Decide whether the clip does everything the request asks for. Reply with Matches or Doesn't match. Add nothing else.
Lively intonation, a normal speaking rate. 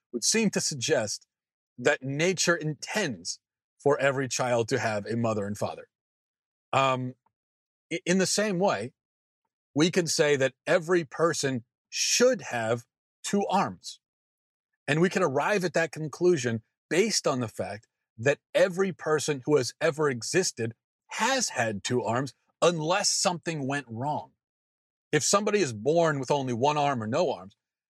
Matches